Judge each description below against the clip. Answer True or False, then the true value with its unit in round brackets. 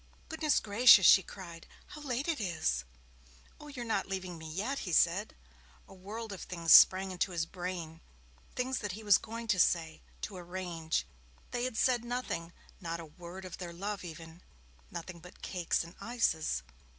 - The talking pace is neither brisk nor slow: True (175 wpm)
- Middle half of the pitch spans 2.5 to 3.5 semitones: False (4.8 semitones)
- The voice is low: False (185 Hz)